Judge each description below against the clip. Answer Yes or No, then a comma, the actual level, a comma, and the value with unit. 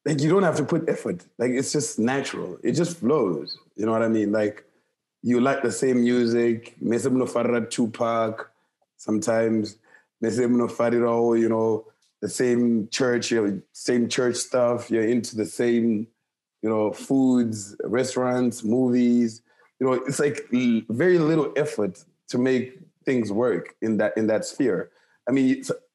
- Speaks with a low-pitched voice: Yes, low, 120 Hz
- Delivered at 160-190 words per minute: No, average, 150 wpm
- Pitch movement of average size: No, narrow, 2.3 semitones